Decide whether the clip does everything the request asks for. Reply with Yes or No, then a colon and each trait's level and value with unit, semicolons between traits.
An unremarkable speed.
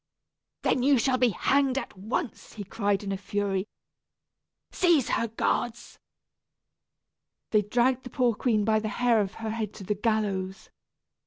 Yes: average, 155 wpm